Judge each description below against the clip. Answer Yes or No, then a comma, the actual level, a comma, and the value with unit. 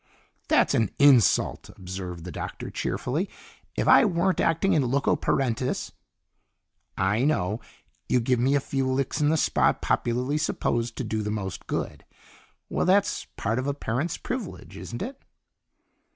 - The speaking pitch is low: Yes, low, 130 Hz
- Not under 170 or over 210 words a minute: No, average, 155 wpm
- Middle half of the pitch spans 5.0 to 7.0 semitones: Yes, average, 5.3 semitones